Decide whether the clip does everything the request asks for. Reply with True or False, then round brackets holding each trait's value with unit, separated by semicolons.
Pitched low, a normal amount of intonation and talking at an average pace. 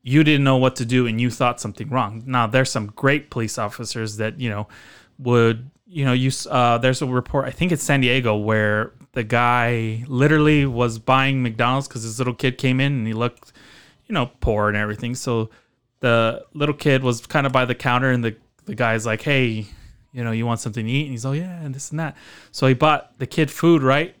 False (125 Hz; 3.0 semitones; 230 wpm)